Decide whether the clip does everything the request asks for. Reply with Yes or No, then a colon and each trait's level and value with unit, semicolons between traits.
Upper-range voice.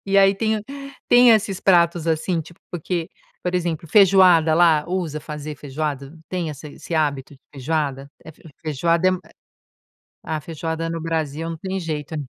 No: medium, 165 Hz